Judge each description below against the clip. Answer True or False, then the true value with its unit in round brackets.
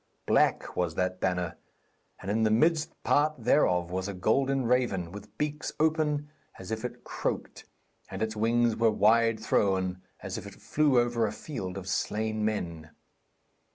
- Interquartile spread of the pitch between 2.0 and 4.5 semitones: False (5.1 semitones)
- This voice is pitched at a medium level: False (110 Hz)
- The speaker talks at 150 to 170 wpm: True (160 wpm)